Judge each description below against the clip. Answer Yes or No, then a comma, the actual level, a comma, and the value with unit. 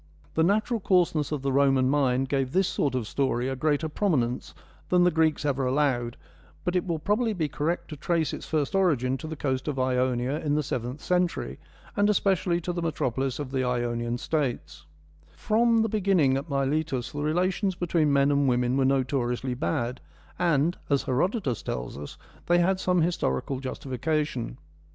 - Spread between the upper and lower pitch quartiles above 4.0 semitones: Yes, average, 5.1 semitones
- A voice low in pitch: No, medium, 145 Hz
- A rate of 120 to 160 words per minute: No, average, 175 wpm